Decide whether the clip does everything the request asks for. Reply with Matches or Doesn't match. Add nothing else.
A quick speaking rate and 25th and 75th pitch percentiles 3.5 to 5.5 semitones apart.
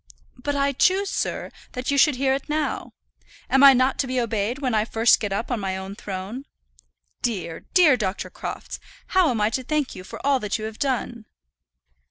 Matches